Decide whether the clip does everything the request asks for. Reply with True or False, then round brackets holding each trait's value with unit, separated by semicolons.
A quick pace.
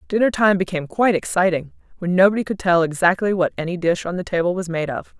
True (220 wpm)